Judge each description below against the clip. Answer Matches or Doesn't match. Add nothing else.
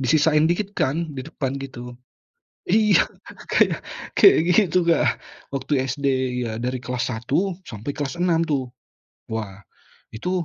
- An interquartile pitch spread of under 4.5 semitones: Doesn't match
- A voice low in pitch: Doesn't match